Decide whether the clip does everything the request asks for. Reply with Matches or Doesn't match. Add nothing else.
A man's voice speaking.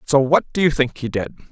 Matches